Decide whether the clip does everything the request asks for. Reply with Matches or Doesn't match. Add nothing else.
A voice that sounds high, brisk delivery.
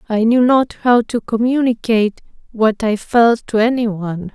Doesn't match